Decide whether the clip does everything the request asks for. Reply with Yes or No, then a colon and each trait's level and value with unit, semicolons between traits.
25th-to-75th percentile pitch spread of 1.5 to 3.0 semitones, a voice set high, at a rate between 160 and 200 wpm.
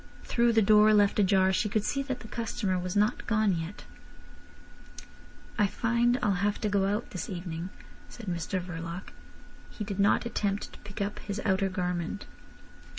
Yes: narrow, 2.6 semitones; high, 200 Hz; average, 170 wpm